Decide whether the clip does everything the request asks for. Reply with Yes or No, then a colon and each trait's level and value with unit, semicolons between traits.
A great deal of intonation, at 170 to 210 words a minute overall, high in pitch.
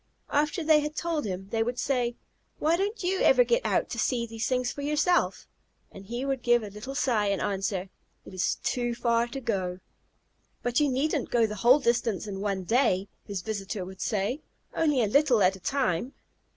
Yes: wide, 6.0 semitones; average, 200 wpm; high, 240 Hz